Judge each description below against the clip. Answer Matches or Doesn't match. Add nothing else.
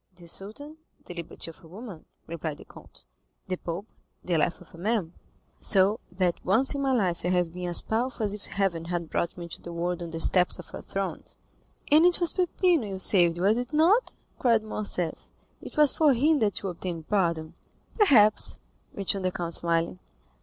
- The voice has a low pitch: Doesn't match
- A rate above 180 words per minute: Matches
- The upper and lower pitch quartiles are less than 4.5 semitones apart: Doesn't match